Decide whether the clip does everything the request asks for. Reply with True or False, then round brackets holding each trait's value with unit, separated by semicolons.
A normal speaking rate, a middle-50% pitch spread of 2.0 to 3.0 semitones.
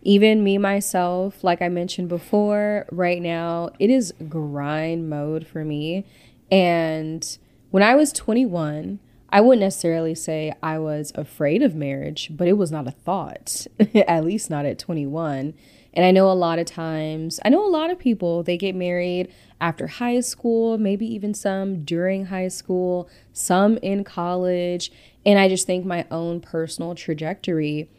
False (165 wpm; 3.6 semitones)